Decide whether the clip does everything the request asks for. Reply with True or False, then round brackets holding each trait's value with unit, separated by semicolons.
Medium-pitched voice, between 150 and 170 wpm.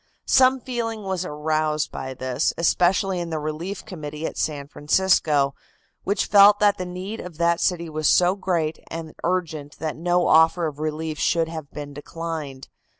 True (165 Hz; 165 wpm)